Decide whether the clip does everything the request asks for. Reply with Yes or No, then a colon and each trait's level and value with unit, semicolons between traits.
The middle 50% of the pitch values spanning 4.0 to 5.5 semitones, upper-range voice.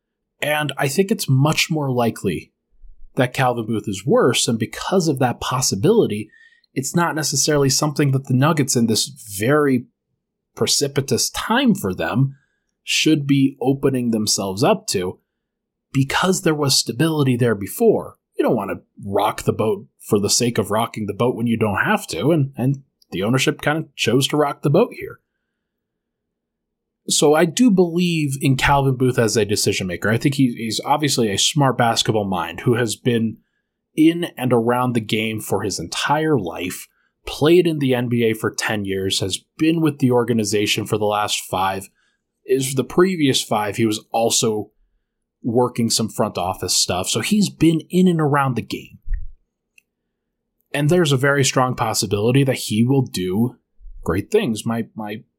No: average, 5.2 semitones; low, 130 Hz